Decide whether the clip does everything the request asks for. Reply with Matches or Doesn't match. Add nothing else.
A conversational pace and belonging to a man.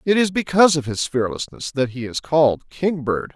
Matches